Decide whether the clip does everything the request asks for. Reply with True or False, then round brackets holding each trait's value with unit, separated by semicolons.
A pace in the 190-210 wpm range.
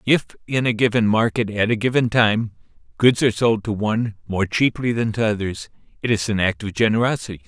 True (200 wpm)